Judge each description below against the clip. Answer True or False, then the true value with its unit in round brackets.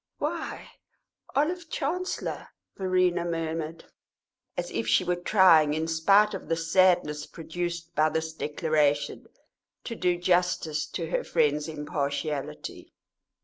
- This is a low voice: False (165 Hz)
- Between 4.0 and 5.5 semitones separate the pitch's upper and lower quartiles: False (3.0 semitones)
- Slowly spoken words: True (115 wpm)